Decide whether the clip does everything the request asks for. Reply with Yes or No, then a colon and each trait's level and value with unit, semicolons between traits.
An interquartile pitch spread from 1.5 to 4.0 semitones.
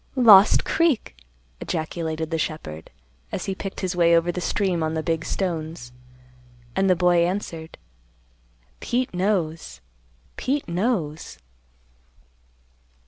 Yes: average, 3.3 semitones